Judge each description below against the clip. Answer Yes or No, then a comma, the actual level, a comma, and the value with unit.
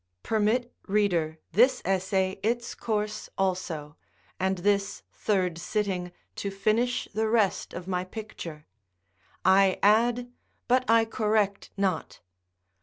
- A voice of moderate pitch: No, high, 200 Hz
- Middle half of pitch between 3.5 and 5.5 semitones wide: No, average, 2.9 semitones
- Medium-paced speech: No, slow, 110 wpm